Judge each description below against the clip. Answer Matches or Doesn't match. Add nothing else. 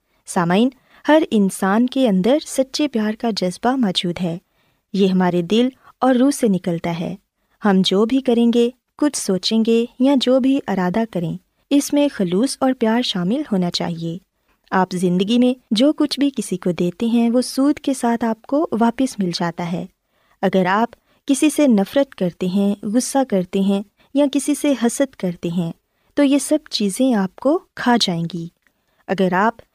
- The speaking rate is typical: Matches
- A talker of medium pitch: Doesn't match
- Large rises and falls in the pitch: Matches